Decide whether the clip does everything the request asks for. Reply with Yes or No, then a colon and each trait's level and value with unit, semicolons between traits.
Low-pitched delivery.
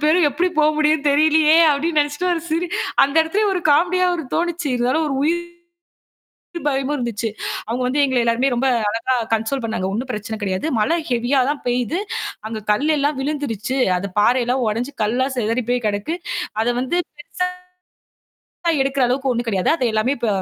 No: very high, 270 Hz